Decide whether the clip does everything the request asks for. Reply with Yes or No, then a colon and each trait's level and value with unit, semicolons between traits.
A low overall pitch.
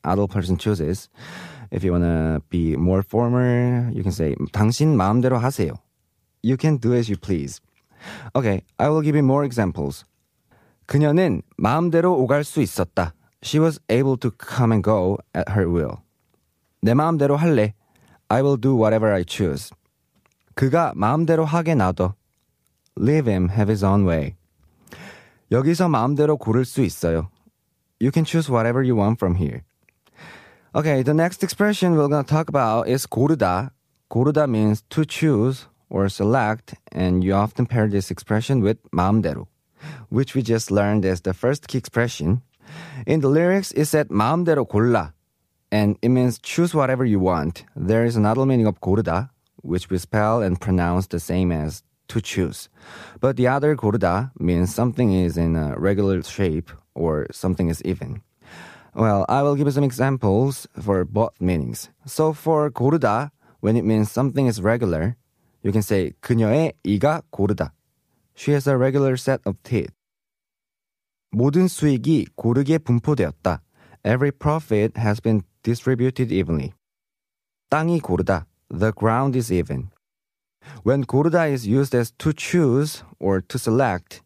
Yes: low, 115 Hz